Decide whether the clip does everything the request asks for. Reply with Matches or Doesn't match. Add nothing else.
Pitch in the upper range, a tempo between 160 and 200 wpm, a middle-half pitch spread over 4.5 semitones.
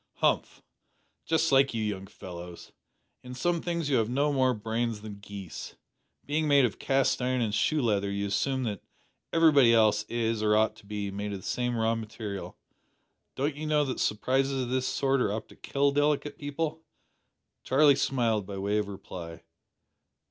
Doesn't match